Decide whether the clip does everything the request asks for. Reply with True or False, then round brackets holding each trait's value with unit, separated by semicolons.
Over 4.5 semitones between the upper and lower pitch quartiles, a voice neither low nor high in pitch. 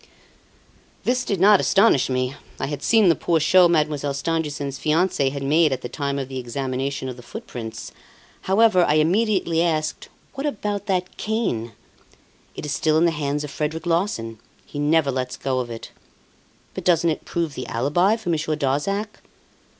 True (5.0 semitones; 155 Hz)